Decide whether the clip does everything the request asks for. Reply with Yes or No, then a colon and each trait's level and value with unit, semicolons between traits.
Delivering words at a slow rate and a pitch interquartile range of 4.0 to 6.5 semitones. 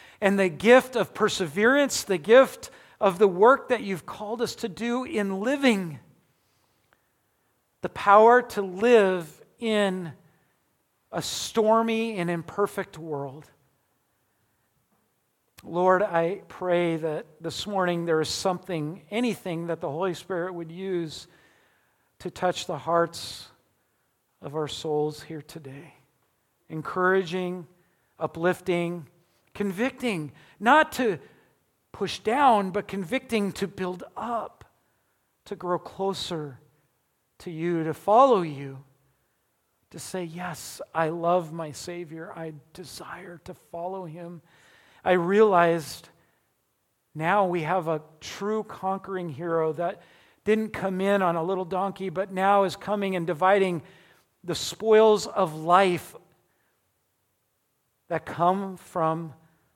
No: slow, 115 wpm; average, 3.5 semitones